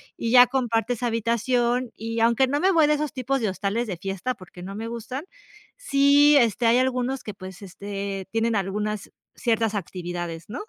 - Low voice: No, high, 230 Hz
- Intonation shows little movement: No, average, 4.2 semitones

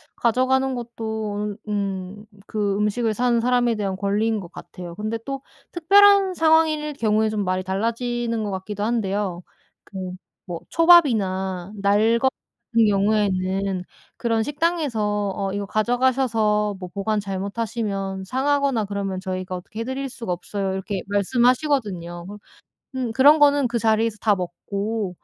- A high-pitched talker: Yes, high, 215 Hz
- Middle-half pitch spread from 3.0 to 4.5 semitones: Yes, average, 3.9 semitones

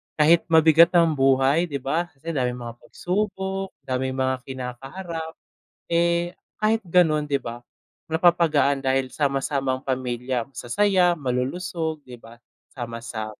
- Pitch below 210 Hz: Yes, medium, 140 Hz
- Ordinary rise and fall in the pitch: Yes, average, 4.7 semitones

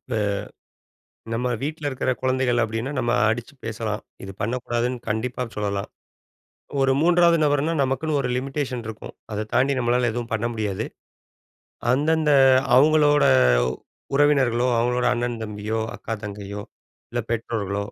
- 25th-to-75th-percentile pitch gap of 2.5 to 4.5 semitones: Yes, average, 3.3 semitones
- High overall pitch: No, low, 120 Hz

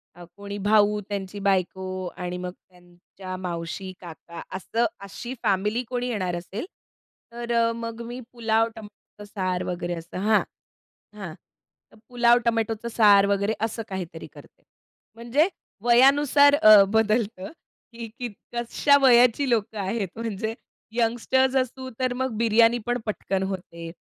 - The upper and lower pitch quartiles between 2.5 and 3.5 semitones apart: No, average, 3.9 semitones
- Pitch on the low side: No, high, 215 Hz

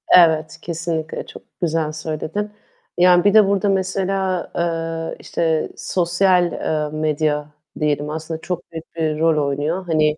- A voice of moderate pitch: Yes, medium, 165 Hz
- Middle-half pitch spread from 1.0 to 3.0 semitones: Yes, narrow, 2.6 semitones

